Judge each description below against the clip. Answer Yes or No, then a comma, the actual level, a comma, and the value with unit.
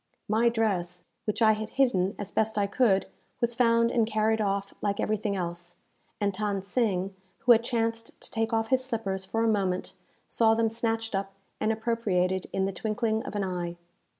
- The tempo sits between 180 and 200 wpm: Yes, average, 185 wpm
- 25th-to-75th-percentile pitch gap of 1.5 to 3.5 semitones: Yes, average, 2.8 semitones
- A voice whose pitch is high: Yes, high, 215 Hz